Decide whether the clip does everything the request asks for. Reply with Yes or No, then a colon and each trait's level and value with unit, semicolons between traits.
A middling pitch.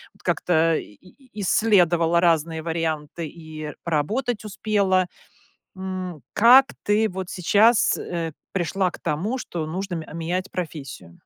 Yes: medium, 175 Hz